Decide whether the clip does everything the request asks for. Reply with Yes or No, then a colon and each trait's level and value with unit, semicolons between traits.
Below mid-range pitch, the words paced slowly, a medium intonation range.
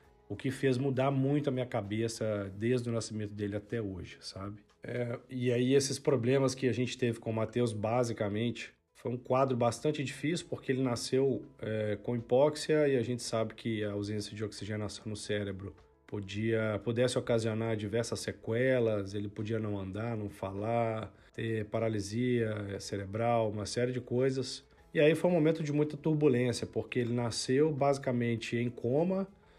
No: low, 115 Hz; average, 165 wpm; average, 3.3 semitones